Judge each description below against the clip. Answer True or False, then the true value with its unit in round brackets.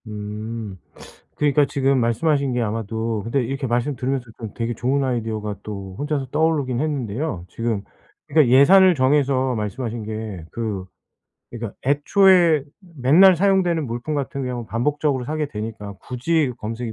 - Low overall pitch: True (125 Hz)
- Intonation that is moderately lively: True (4.6 semitones)